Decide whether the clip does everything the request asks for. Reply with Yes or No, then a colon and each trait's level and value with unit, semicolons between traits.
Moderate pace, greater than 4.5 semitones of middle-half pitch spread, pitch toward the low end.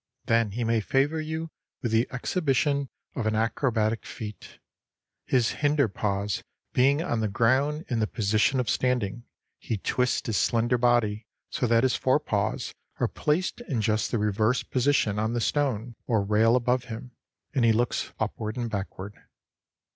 No: average, 160 wpm; average, 3.2 semitones; low, 120 Hz